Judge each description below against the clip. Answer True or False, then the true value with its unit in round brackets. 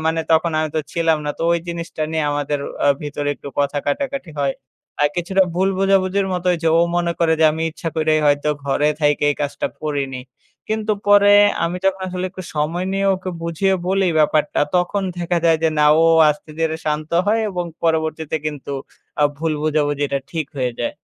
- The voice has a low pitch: False (160 Hz)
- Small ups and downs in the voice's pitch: False (3.3 semitones)